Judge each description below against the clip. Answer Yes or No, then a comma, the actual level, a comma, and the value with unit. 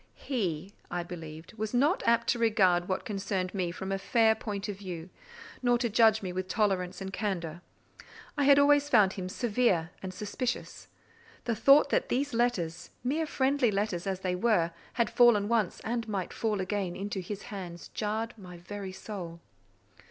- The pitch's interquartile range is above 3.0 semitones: Yes, average, 4.3 semitones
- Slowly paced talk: No, average, 175 wpm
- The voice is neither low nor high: No, high, 205 Hz